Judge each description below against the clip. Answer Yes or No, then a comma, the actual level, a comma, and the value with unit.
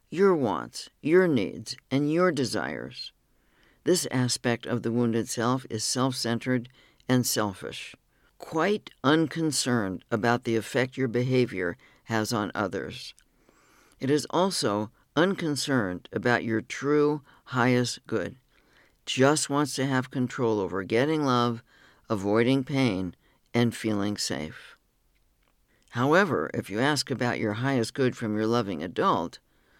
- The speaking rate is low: Yes, slow, 125 wpm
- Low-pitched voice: Yes, low, 125 Hz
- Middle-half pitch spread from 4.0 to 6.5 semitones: No, average, 3.2 semitones